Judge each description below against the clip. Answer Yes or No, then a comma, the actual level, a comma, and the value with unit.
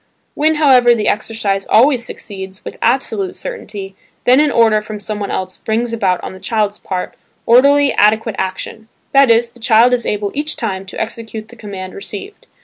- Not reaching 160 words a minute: No, average, 175 wpm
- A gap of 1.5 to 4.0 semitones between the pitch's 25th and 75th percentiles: Yes, average, 3.2 semitones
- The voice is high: Yes, high, 220 Hz